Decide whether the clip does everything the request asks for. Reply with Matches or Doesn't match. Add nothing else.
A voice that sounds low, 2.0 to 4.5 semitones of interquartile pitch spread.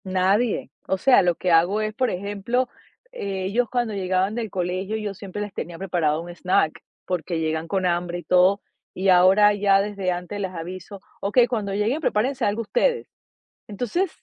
Doesn't match